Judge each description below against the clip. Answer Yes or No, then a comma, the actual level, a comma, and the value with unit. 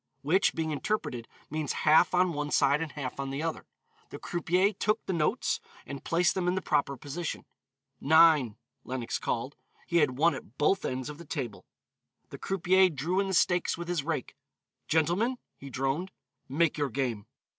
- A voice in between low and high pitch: Yes, medium, 155 Hz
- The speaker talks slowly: No, average, 180 wpm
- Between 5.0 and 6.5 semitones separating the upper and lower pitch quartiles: No, average, 4.3 semitones